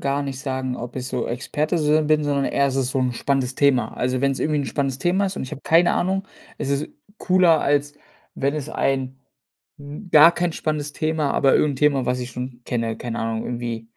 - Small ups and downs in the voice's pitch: No, average, 3.1 semitones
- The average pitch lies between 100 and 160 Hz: Yes, medium, 140 Hz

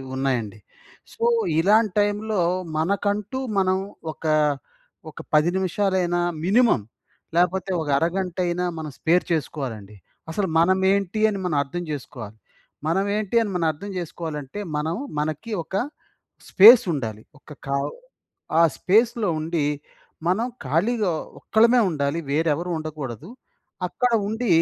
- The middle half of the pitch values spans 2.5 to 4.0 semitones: No, average, 5.2 semitones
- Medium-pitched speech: Yes, medium, 175 Hz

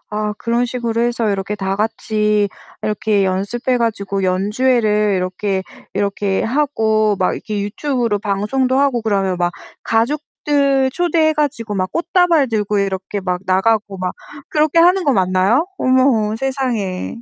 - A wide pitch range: No, average, 4.7 semitones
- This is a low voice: No, high, 215 Hz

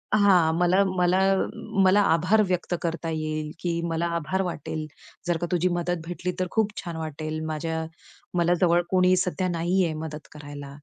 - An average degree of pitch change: No, narrow, 2.3 semitones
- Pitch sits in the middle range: Yes, medium, 170 Hz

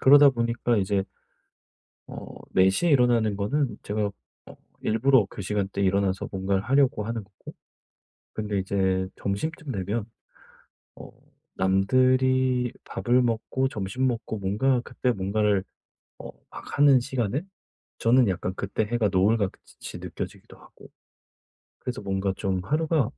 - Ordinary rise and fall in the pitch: Yes, average, 4.6 semitones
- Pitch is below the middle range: Yes, low, 110 Hz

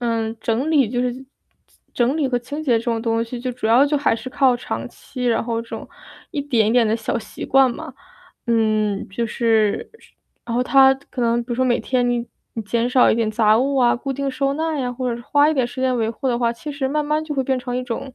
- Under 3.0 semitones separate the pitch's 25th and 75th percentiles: Yes, narrow, 2.6 semitones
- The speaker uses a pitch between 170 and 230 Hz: No, high, 245 Hz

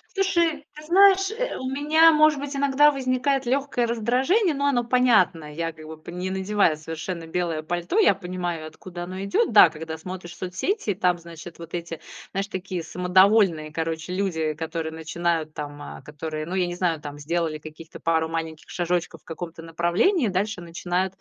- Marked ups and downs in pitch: Yes, wide, 7.1 semitones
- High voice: No, medium, 180 Hz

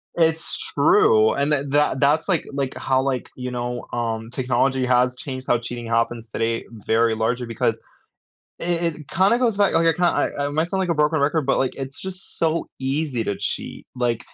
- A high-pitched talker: No, low, 135 Hz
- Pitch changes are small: No, average, 5.0 semitones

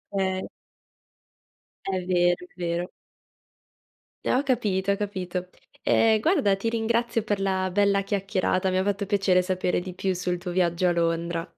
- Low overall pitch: No, high, 190 Hz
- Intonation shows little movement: Yes, narrow, 2.2 semitones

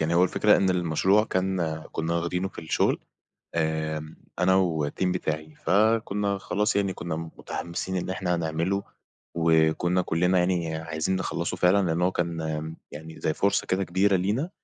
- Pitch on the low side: Yes, very low, 90 Hz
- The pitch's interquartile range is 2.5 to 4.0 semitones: Yes, average, 2.8 semitones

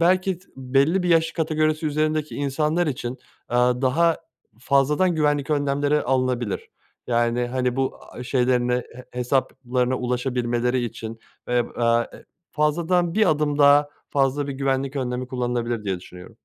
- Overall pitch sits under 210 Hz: Yes, low, 135 Hz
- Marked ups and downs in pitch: No, average, 3.5 semitones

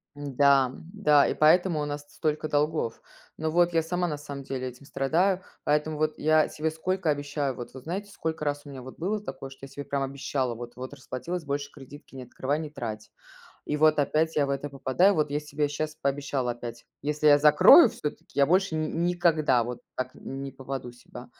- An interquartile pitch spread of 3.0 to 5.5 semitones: No, narrow, 2.6 semitones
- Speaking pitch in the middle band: Yes, medium, 145 Hz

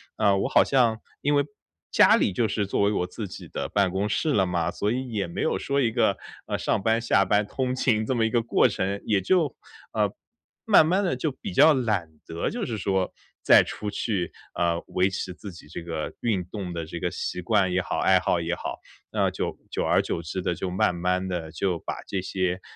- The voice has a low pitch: Yes, low, 100 Hz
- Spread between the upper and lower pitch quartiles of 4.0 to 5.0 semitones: Yes, average, 4.4 semitones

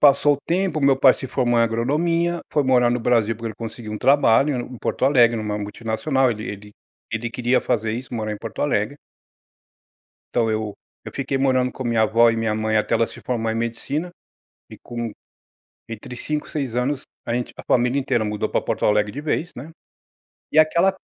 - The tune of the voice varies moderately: Yes, average, 3.6 semitones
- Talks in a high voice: No, low, 120 Hz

